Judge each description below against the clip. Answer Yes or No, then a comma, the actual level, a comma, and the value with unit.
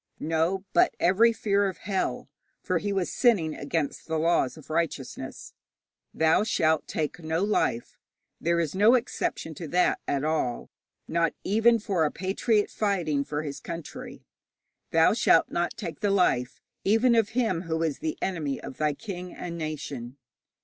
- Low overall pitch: No, medium, 170 Hz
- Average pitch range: Yes, average, 4.3 semitones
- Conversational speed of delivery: Yes, average, 160 wpm